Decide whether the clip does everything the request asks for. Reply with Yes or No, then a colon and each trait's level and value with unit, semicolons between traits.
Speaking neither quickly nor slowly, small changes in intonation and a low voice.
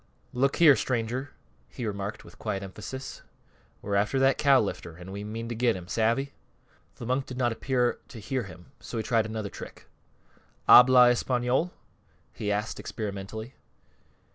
No: average, 160 wpm; average, 3.9 semitones; low, 115 Hz